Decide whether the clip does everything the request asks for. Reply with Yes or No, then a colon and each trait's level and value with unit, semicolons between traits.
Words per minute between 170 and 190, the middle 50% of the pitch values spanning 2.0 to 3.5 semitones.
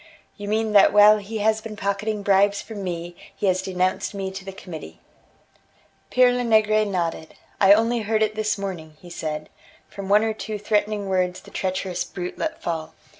Yes: average, 180 wpm; average, 2.7 semitones